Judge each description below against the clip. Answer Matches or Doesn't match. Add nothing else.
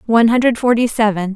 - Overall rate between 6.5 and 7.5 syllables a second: Matches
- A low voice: Doesn't match